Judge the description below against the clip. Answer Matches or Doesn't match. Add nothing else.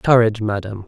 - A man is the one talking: Matches